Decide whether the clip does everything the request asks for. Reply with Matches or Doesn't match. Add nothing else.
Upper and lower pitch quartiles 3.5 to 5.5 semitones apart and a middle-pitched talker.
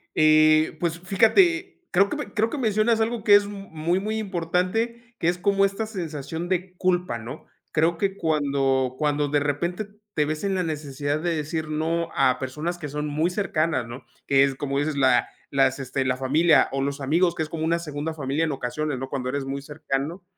Matches